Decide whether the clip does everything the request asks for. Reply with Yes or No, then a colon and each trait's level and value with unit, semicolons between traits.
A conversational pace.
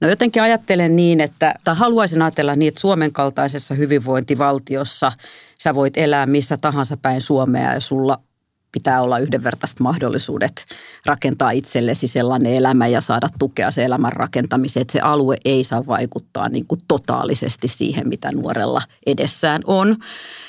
Yes: average, 145 wpm